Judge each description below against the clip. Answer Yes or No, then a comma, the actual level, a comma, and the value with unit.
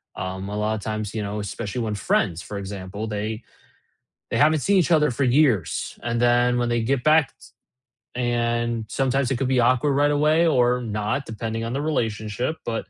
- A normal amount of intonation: Yes, average, 4.0 semitones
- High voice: No, low, 120 Hz